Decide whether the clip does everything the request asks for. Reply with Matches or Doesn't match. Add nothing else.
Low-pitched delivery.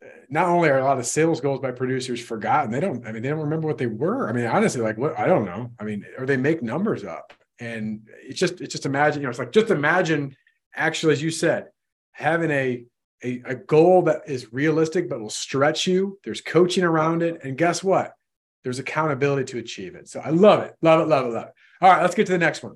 Doesn't match